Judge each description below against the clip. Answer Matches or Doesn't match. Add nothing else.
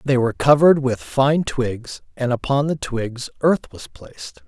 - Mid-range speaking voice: Doesn't match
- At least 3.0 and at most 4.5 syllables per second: Matches